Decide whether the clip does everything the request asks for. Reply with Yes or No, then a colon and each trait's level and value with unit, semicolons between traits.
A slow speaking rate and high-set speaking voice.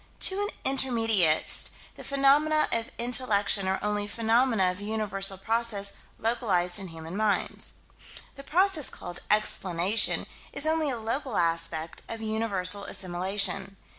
Yes: slow, 125 wpm; high, 215 Hz